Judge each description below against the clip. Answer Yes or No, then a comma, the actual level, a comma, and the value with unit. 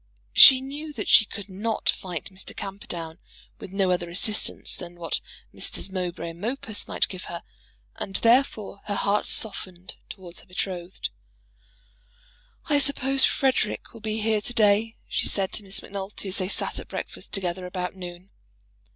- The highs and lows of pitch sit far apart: No, average, 3.3 semitones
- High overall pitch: Yes, high, 195 Hz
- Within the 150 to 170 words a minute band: Yes, average, 160 wpm